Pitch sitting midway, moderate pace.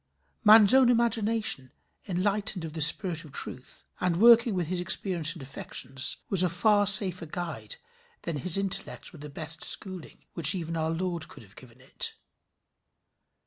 Yes: medium, 180 Hz; average, 160 wpm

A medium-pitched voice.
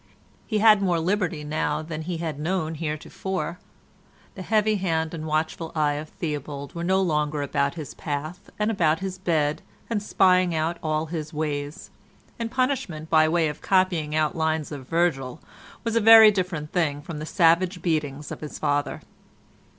Yes: medium, 160 Hz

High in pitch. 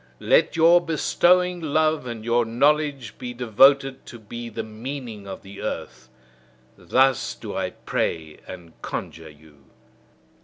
No: low, 120 Hz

